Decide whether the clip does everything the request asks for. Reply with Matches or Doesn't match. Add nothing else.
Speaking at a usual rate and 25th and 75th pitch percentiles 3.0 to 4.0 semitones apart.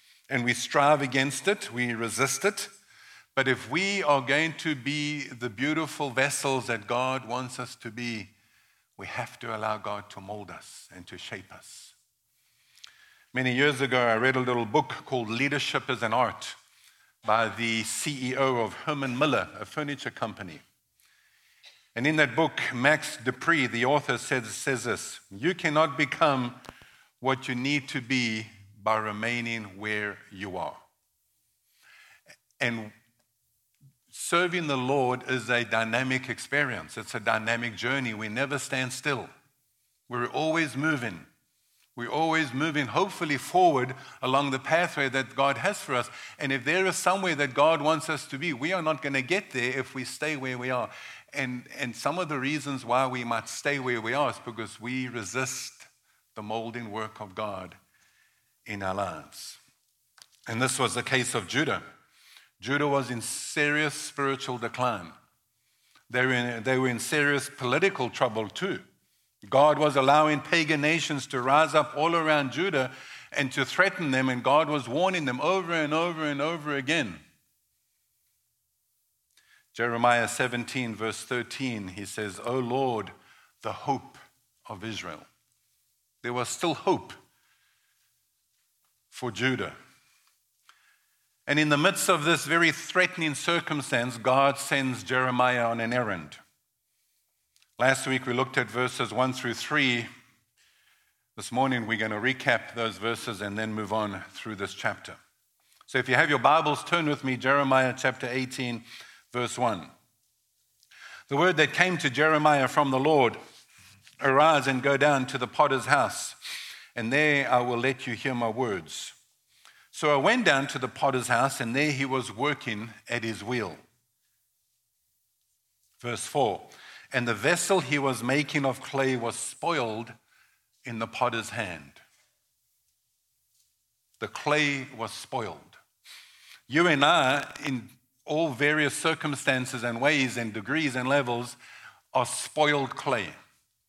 Matches